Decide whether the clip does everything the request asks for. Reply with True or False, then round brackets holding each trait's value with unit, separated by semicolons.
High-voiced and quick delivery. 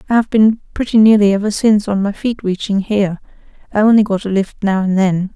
True (205 Hz; 225 wpm)